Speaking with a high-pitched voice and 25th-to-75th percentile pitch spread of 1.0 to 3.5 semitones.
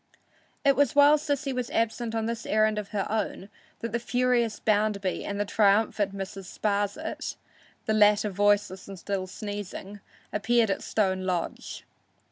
Yes: high, 210 Hz; narrow, 2.6 semitones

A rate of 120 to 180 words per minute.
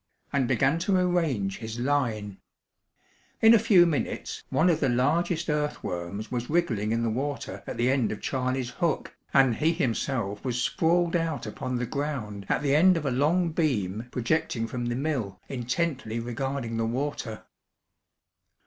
Yes: average, 160 wpm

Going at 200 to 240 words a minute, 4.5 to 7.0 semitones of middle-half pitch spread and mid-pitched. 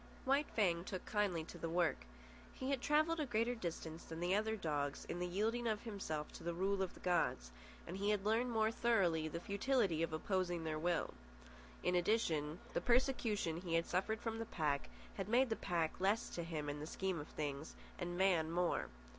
Yes: fast, 205 wpm; average, 5.1 semitones; medium, 180 Hz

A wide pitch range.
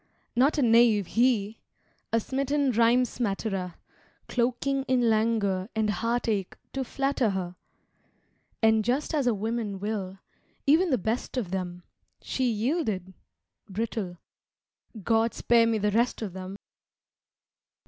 No: average, 3.8 semitones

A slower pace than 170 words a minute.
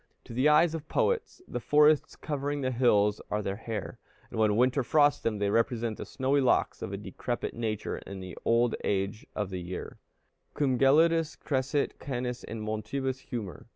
No: average, 180 wpm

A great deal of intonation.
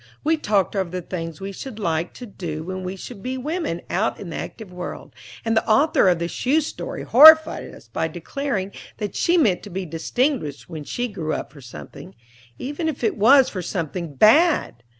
Yes: wide, 7.2 semitones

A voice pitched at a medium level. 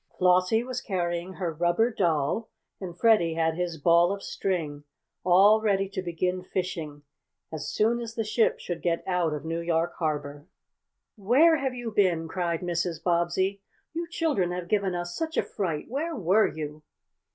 Yes: medium, 180 Hz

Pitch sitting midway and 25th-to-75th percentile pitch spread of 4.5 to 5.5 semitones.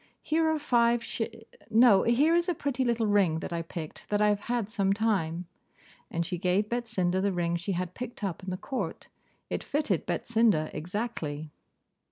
No: high, 205 Hz; average, 5.1 semitones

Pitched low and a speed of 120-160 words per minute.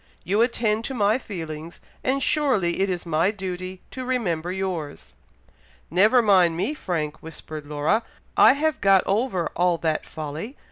No: medium, 185 Hz; average, 150 wpm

